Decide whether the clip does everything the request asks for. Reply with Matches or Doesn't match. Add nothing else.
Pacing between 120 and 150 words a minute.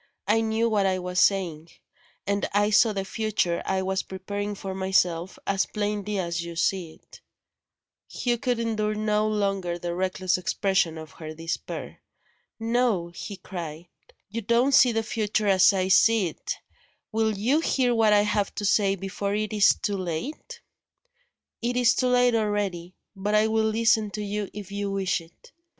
Doesn't match